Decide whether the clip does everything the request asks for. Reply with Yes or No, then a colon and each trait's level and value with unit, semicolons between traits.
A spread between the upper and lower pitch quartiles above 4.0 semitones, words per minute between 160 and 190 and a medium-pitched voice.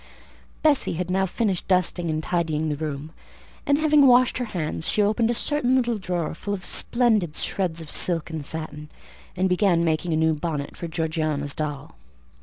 Yes: average, 4.9 semitones; average, 180 wpm; medium, 170 Hz